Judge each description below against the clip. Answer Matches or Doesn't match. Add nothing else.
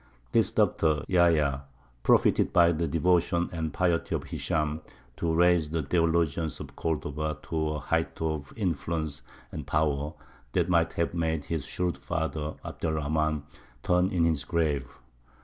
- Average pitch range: Doesn't match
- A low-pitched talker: Matches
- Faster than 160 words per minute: Doesn't match